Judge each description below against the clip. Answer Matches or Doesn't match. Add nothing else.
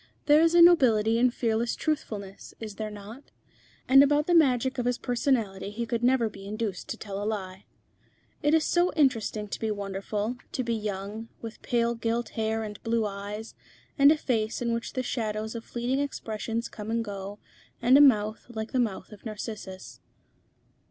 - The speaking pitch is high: Matches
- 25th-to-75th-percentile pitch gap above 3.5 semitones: Doesn't match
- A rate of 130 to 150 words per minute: Doesn't match